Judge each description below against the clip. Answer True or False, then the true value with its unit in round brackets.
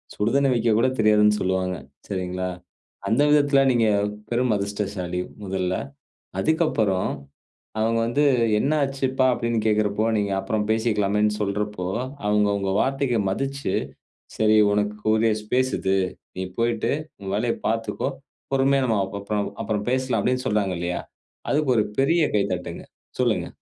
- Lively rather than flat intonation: False (3.9 semitones)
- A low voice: True (110 Hz)